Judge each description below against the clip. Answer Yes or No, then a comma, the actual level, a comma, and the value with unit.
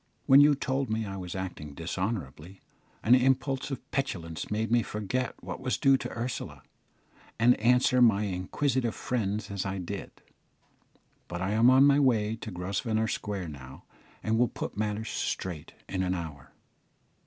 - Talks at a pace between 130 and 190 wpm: Yes, average, 160 wpm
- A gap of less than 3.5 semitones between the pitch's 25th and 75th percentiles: No, average, 5.0 semitones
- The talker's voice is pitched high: No, low, 105 Hz